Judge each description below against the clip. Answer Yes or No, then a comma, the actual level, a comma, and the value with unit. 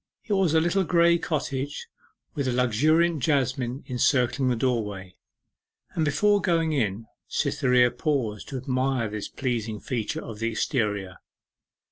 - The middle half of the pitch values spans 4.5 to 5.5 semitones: Yes, average, 5.2 semitones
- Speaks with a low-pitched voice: Yes, low, 130 Hz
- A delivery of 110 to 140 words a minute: Yes, slow, 135 wpm